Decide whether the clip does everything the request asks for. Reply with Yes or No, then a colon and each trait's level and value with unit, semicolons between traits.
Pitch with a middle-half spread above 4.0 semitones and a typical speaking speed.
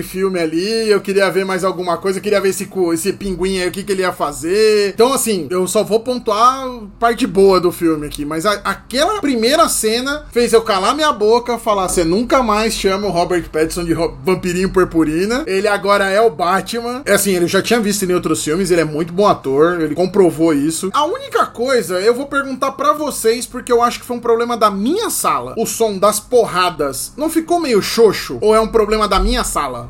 No: average, 4.8 semitones; fast, 220 wpm